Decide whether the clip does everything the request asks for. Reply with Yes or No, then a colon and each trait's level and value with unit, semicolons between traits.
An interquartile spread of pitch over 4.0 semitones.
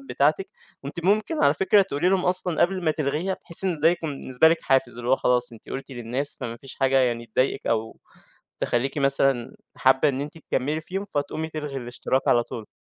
Yes: average, 4.7 semitones